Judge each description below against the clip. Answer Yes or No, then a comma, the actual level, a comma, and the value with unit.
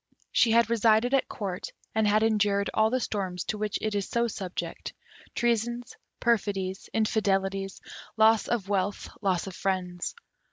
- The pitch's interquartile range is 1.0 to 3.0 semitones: Yes, narrow, 2.6 semitones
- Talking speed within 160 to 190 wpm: No, average, 150 wpm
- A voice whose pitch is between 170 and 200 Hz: No, high, 210 Hz